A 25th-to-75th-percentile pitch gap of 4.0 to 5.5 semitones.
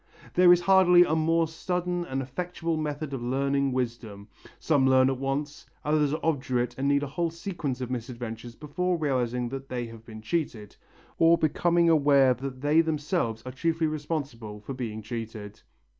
Yes: average, 4.8 semitones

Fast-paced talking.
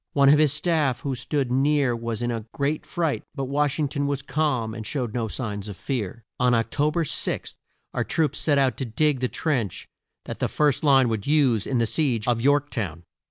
Yes: fast, 220 wpm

